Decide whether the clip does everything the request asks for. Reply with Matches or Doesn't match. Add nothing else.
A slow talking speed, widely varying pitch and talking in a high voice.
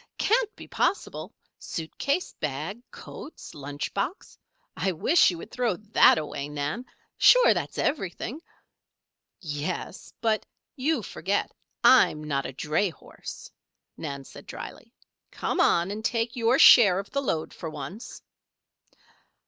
Matches